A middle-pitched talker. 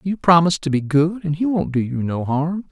Yes: medium, 160 Hz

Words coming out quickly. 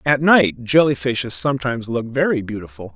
No: average, 160 wpm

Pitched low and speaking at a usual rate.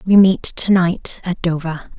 No: medium, 175 Hz; average, 180 wpm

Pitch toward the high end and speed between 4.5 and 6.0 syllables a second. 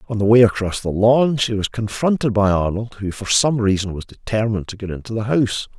No: low, 110 Hz; 5.8 syllables/s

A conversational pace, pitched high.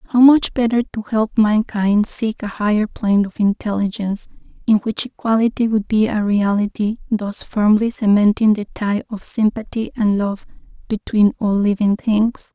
Yes: average, 155 wpm; high, 215 Hz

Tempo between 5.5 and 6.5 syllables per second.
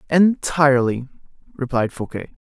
No: 4.7 syllables/s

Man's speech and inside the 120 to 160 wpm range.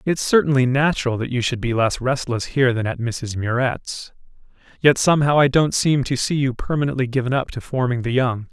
No: male; fast, 205 wpm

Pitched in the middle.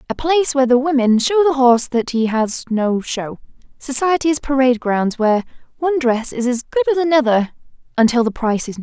No: very high, 260 Hz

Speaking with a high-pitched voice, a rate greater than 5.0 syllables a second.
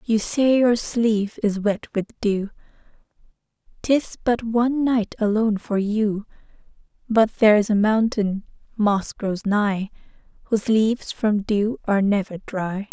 No: high, 215 Hz; 4.2 syllables/s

